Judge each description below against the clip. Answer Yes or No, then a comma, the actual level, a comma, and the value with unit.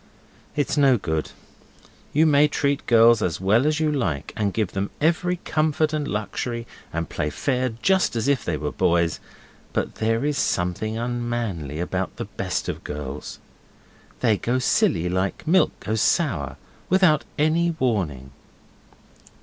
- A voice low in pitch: Yes, low, 115 Hz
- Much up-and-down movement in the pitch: Yes, wide, 8.6 semitones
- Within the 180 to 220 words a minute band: No, average, 150 wpm